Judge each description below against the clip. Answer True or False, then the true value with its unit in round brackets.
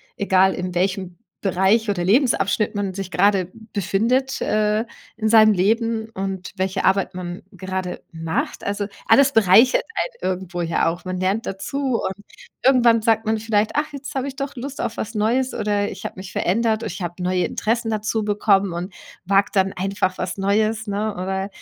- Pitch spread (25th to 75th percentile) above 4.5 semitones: False (3.1 semitones)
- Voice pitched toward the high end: True (200 Hz)